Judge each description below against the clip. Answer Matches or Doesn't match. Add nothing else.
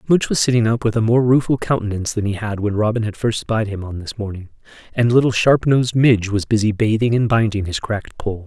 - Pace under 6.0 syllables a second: Doesn't match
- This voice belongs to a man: Matches